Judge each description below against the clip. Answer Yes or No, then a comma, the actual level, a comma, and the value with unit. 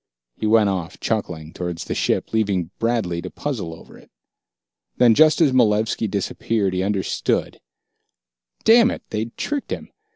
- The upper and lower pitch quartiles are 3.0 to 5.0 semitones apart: Yes, average, 4.2 semitones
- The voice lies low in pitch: Yes, low, 105 Hz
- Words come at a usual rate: Yes, average, 150 wpm